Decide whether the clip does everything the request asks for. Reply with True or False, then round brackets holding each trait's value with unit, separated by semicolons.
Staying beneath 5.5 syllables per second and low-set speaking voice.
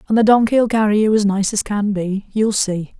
False (5.1 syllables/s; 210 Hz)